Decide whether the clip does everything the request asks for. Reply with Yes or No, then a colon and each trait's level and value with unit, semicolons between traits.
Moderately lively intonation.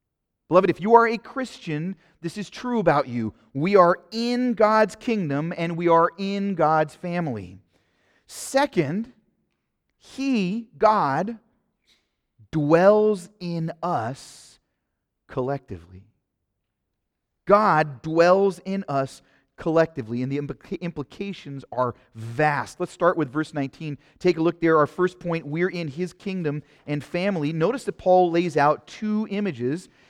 No: wide, 5.9 semitones